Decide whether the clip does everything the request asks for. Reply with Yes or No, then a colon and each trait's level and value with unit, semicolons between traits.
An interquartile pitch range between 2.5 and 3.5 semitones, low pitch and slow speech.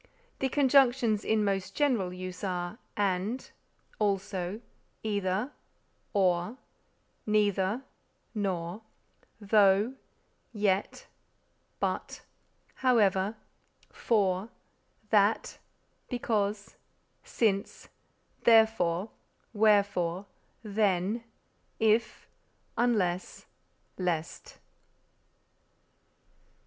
No: average, 2.9 semitones; high, 205 Hz; slow, 60 wpm